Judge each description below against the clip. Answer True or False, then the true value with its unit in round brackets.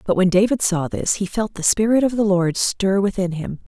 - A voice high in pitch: True (195 Hz)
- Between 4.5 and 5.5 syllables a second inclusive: True (5.2 syllables/s)